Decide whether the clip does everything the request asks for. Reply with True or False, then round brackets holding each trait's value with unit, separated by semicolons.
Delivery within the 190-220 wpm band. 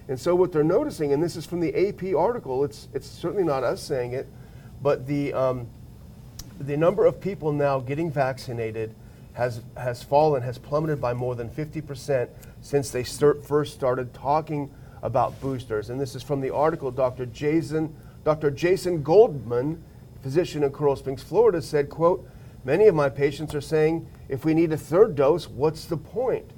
False (180 wpm)